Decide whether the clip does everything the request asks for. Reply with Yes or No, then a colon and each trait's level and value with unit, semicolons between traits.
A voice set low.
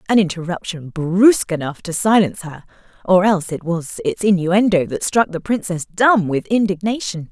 No: high, 190 Hz